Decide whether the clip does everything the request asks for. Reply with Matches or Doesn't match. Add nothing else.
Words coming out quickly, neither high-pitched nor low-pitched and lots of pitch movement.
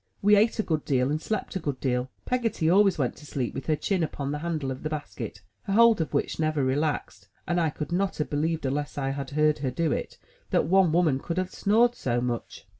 Doesn't match